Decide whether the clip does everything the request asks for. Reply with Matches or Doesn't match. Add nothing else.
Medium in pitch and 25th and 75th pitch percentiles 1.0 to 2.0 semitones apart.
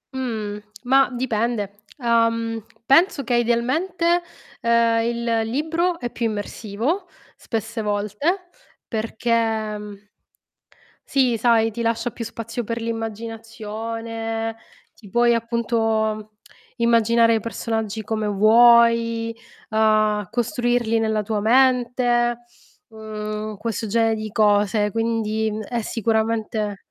Doesn't match